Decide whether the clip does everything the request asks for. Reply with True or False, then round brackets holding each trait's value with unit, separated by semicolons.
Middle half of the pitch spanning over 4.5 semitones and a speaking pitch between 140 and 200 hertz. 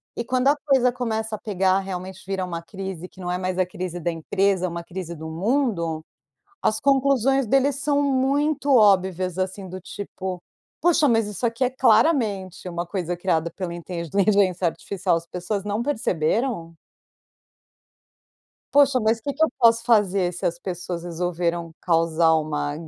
True (5.1 semitones; 190 Hz)